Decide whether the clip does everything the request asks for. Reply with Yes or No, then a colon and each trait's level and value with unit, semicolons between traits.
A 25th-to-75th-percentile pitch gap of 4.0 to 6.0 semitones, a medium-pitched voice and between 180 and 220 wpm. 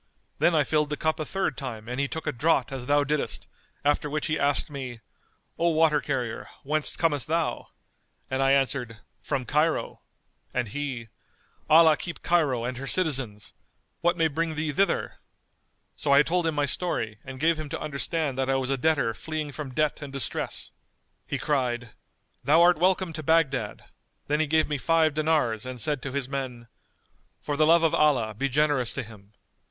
No: average, 3.3 semitones; medium, 145 Hz; average, 190 wpm